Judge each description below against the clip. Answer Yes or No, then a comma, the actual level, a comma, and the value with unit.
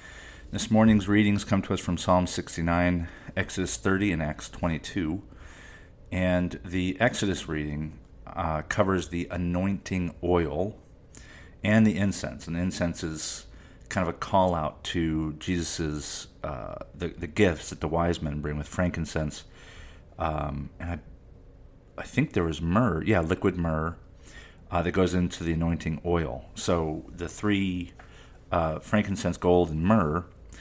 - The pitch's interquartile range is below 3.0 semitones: Yes, narrow, 2.6 semitones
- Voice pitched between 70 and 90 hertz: Yes, very low, 85 Hz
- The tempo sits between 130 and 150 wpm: Yes, average, 145 wpm